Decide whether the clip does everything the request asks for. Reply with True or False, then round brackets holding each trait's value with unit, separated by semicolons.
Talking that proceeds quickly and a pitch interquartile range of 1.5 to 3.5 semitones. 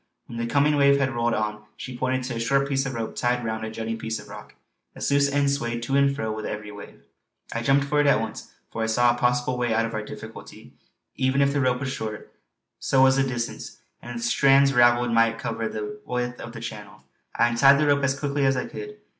True (245 wpm; 3.1 semitones)